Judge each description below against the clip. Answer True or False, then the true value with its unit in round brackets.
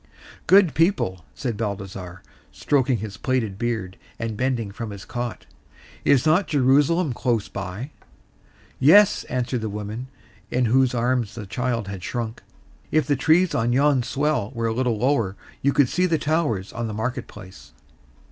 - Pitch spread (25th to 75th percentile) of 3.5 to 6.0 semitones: True (4.7 semitones)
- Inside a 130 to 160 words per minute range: True (155 wpm)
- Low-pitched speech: True (120 Hz)